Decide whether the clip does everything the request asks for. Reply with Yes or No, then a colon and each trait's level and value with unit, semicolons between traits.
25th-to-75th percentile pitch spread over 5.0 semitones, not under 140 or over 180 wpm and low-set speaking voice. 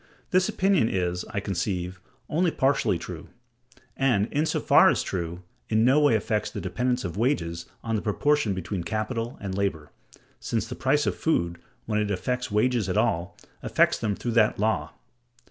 Yes: wide, 5.5 semitones; average, 175 wpm; low, 105 Hz